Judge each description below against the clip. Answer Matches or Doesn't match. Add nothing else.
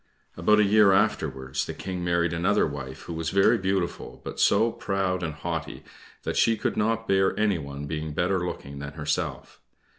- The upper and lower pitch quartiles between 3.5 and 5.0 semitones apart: Matches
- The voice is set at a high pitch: Doesn't match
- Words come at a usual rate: Matches